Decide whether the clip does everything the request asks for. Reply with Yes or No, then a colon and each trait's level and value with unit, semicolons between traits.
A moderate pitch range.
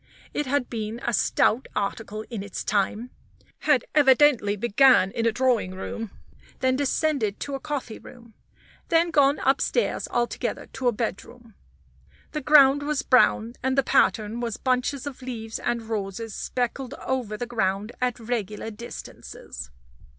Yes: average, 3.6 semitones